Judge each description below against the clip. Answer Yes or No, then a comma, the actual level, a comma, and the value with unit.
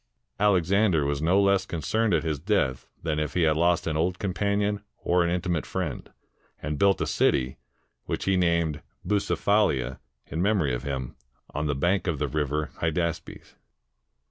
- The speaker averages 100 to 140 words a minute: No, average, 165 wpm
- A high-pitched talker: No, very low, 85 Hz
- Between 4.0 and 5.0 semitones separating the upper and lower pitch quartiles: Yes, average, 4.4 semitones